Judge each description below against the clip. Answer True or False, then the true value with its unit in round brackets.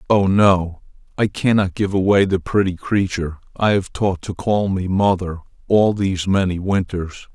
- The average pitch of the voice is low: True (95 Hz)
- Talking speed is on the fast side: False (165 wpm)